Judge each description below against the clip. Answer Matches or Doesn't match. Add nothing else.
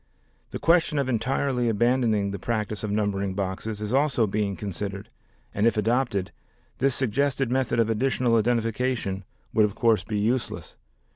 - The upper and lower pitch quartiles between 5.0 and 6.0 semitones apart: Doesn't match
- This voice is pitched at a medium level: Doesn't match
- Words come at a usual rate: Matches